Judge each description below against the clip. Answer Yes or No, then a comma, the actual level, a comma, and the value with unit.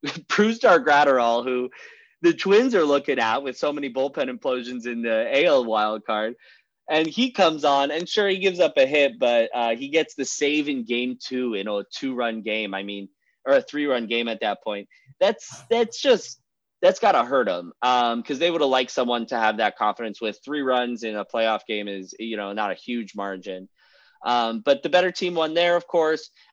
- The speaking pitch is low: Yes, low, 125 Hz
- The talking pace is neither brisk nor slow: No, fast, 210 wpm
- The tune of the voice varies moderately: No, wide, 6.0 semitones